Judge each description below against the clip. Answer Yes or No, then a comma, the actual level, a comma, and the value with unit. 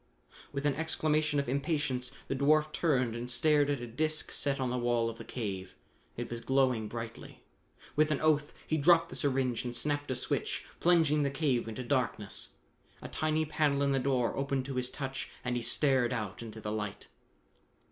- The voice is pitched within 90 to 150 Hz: Yes, low, 135 Hz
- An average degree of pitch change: Yes, average, 3.7 semitones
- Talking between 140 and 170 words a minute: No, average, 190 wpm